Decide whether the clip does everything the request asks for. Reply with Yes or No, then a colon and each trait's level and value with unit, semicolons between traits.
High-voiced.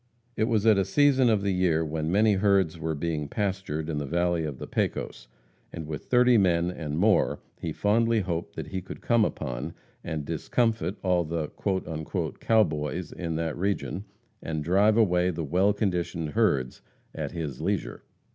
No: very low, 90 Hz